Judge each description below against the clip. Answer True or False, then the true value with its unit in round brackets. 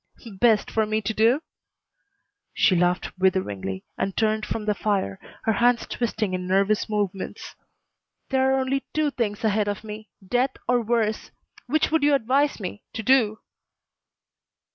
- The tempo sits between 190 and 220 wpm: False (150 wpm)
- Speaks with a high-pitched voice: True (220 Hz)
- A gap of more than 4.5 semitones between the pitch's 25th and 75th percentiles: False (3.5 semitones)